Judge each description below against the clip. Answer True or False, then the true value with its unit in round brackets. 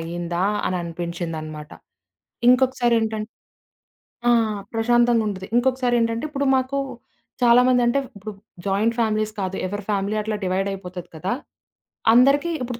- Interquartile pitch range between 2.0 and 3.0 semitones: False (4.7 semitones)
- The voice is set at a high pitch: True (215 Hz)